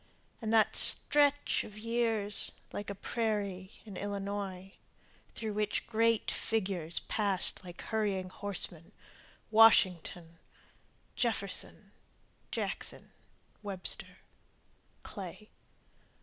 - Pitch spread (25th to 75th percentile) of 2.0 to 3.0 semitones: Yes, average, 2.7 semitones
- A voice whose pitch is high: Yes, high, 205 Hz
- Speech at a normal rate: No, slow, 85 wpm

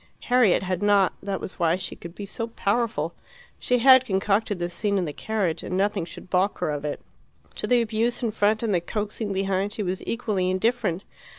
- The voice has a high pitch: Yes, high, 200 Hz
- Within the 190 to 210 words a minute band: Yes, fast, 205 wpm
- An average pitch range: Yes, average, 3.4 semitones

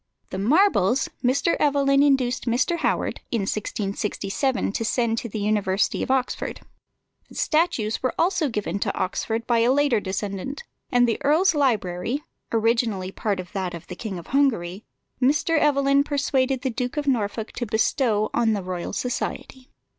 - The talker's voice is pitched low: No, high, 235 Hz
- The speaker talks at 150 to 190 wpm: Yes, average, 160 wpm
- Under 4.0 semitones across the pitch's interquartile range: No, average, 5.0 semitones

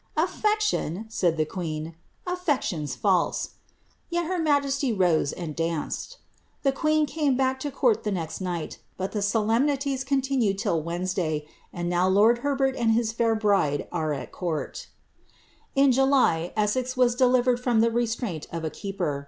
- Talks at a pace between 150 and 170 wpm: Yes, average, 165 wpm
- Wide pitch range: Yes, wide, 7.5 semitones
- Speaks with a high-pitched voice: Yes, high, 225 Hz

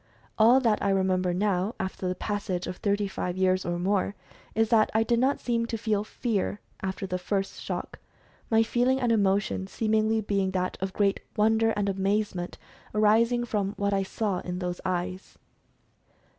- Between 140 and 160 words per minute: No, average, 170 wpm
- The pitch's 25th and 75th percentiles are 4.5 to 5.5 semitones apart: No, average, 2.8 semitones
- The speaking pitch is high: Yes, high, 200 Hz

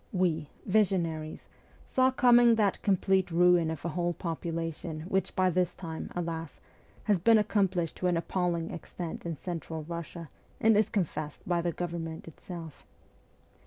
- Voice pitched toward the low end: No, medium, 175 Hz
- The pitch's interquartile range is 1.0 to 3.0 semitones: Yes, narrow, 2.6 semitones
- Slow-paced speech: No, average, 150 wpm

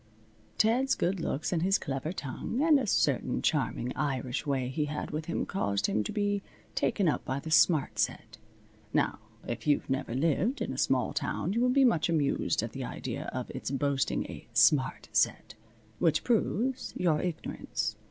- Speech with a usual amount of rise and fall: No, wide, 6.9 semitones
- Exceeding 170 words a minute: Yes, average, 180 wpm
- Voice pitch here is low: No, medium, 155 Hz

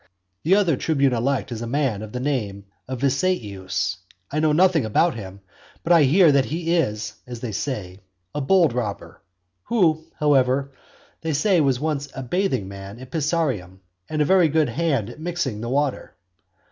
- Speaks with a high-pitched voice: No, medium, 140 Hz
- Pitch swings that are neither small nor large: No, wide, 6.0 semitones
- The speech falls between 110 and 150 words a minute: No, average, 175 wpm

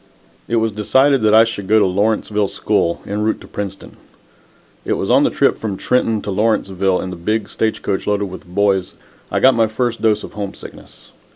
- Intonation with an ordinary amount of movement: No, narrow, 2.3 semitones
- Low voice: Yes, low, 105 Hz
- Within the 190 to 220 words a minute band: Yes, average, 200 wpm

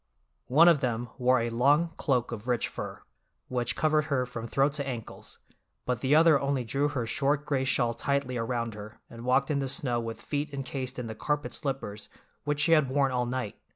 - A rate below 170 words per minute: No, fast, 205 wpm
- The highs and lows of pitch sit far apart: No, average, 3.1 semitones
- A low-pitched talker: Yes, low, 130 Hz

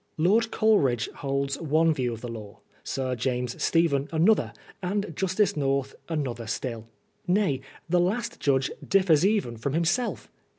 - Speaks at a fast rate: No, average, 140 wpm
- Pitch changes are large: Yes, wide, 6.4 semitones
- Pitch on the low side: No, medium, 150 Hz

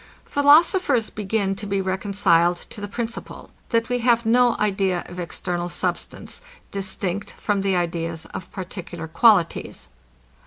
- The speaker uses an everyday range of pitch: Yes, average, 4.3 semitones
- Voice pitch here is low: No, high, 195 Hz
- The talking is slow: Yes, slow, 130 wpm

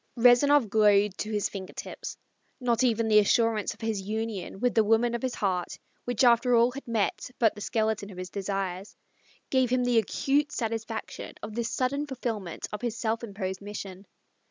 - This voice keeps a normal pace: Yes, average, 180 wpm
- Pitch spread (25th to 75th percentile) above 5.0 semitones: No, average, 3.0 semitones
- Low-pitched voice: No, high, 225 Hz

